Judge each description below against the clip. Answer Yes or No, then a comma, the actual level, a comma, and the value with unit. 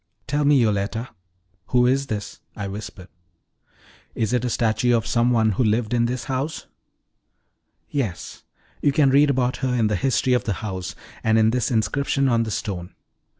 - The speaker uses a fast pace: No, average, 175 wpm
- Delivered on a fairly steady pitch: No, average, 3.3 semitones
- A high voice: No, low, 120 Hz